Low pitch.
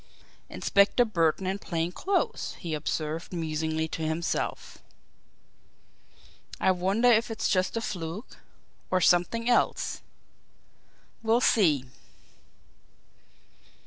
No: medium, 180 Hz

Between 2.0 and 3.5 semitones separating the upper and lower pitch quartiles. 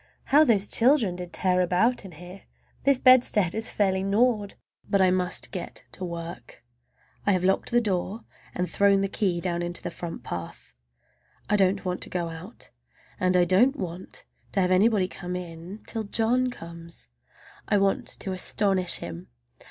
Yes: average, 2.8 semitones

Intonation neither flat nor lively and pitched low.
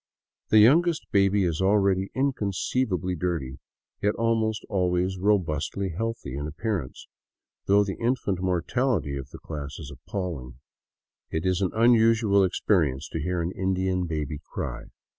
Yes: average, 4.6 semitones; very low, 95 Hz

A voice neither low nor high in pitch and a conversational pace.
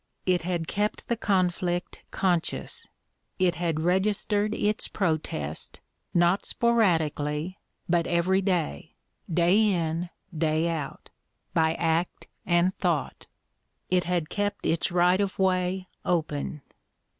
No: medium, 175 Hz; slow, 110 wpm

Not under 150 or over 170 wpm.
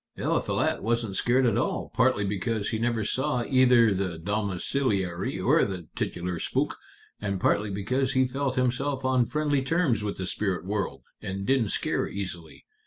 Yes: average, 160 wpm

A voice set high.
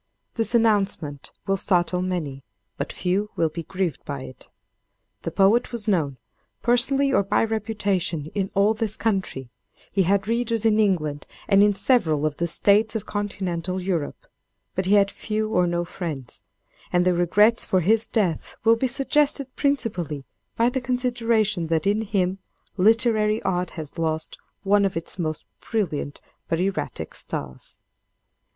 Yes: high, 195 Hz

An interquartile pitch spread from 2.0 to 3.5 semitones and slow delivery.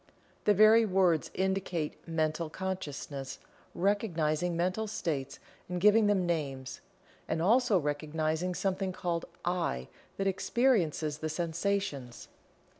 No: average, 4.0 semitones; slow, 110 wpm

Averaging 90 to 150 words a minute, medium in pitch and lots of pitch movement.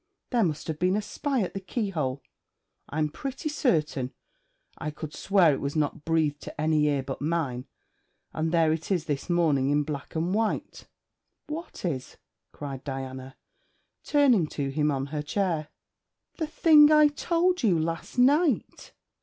No: average, 160 wpm; medium, 160 Hz; wide, 7.0 semitones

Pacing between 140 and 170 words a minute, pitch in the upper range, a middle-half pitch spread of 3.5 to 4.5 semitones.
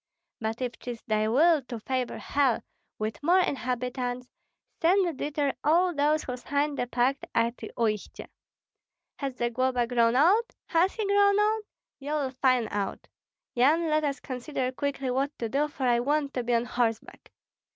Yes: average, 160 wpm; very high, 265 Hz; average, 3.8 semitones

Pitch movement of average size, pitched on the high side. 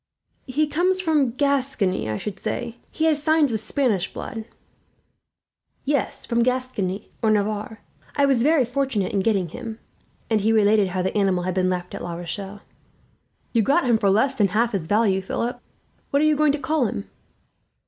No: wide, 5.9 semitones; high, 225 Hz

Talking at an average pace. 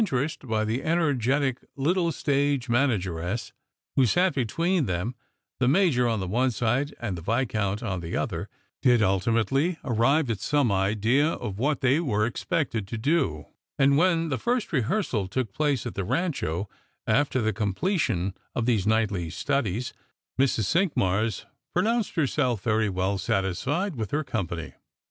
Yes: average, 155 wpm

